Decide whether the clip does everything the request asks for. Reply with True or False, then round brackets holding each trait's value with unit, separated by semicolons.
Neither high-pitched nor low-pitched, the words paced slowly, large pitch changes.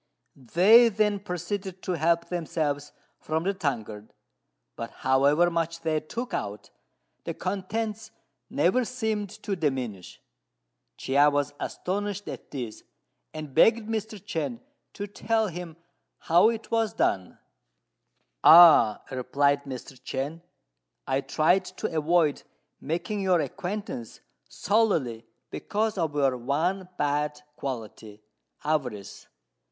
True (165 Hz; 115 wpm; 6.3 semitones)